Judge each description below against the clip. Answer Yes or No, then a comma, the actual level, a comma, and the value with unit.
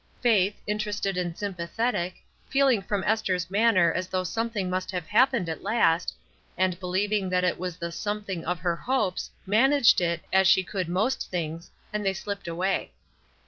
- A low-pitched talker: No, high, 190 Hz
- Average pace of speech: Yes, average, 165 wpm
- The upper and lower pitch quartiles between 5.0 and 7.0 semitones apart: No, average, 2.9 semitones